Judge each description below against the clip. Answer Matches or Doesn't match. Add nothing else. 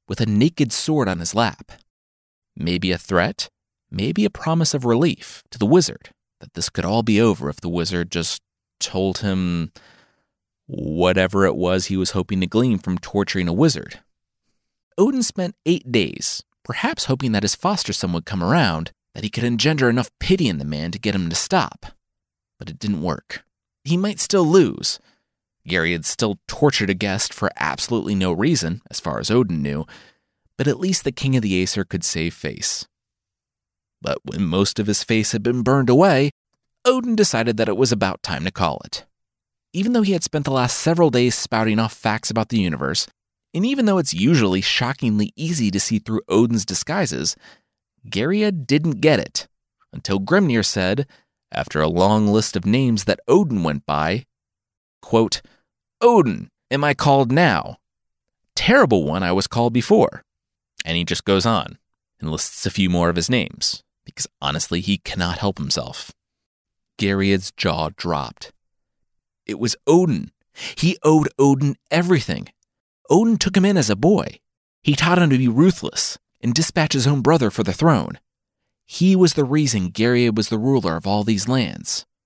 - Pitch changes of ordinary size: Doesn't match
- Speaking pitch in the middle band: Doesn't match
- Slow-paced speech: Doesn't match